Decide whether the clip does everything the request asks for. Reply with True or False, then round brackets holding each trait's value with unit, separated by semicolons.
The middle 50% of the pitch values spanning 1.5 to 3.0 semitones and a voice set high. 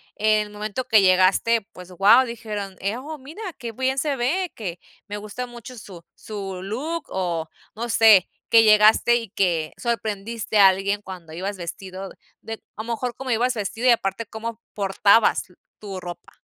False (3.5 semitones; 215 Hz)